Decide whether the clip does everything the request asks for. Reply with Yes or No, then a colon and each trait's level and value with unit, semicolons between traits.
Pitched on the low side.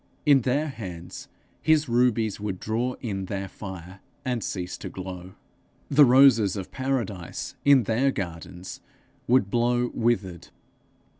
Yes: low, 110 Hz